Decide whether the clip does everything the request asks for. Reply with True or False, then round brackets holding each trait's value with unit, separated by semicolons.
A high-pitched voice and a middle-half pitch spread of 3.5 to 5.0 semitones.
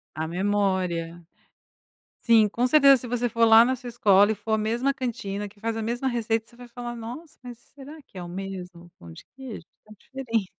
True (225 Hz; 3.9 semitones)